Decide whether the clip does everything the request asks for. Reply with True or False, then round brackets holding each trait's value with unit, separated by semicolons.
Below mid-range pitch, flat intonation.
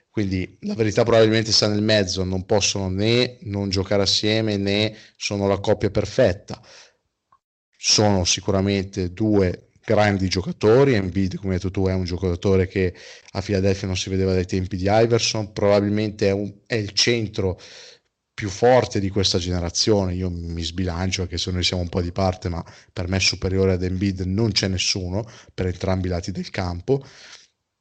True (100 Hz; 2.2 semitones)